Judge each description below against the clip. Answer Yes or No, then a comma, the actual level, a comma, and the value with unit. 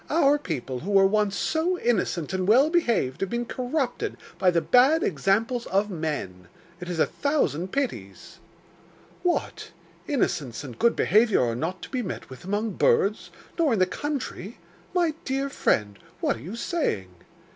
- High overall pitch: Yes, high, 210 Hz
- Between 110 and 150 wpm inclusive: No, average, 165 wpm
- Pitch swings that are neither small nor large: No, wide, 8.2 semitones